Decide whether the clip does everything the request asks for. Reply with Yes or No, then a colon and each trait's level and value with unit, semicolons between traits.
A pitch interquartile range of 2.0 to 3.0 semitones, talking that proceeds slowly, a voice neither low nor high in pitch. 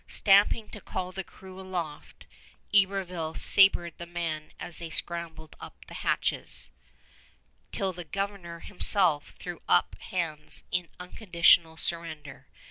Yes: average, 2.7 semitones; slow, 125 wpm; medium, 175 Hz